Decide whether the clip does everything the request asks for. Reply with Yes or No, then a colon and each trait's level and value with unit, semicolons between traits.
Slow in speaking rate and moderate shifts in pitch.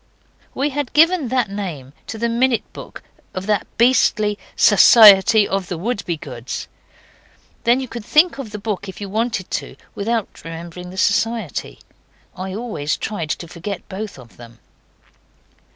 No: average, 150 wpm; average, 4.7 semitones